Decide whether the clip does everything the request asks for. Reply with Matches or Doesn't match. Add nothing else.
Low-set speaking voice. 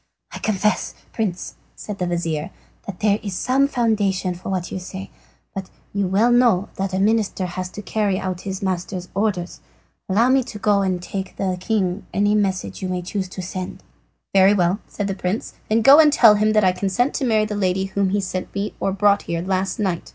Doesn't match